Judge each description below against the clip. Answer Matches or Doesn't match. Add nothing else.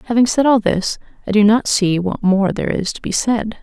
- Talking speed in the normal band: Doesn't match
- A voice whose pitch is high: Matches